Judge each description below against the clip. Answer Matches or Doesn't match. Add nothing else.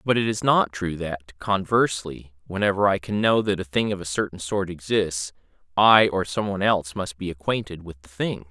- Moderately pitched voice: Doesn't match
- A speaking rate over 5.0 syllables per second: Matches